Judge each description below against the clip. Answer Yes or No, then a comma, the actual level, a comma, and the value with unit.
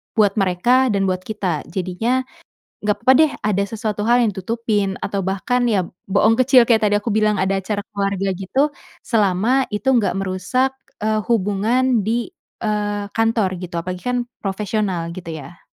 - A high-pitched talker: Yes, high, 210 Hz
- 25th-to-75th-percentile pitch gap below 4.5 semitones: Yes, average, 3.4 semitones